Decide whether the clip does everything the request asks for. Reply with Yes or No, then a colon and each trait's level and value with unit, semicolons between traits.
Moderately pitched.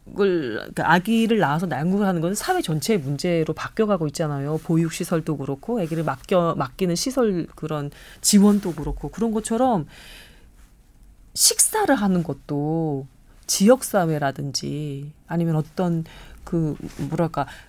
Yes: medium, 165 Hz